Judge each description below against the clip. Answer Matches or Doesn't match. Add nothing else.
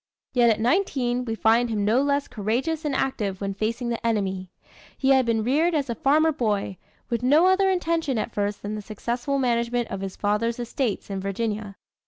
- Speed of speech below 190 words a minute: Doesn't match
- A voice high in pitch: Matches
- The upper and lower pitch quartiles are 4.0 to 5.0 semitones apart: Matches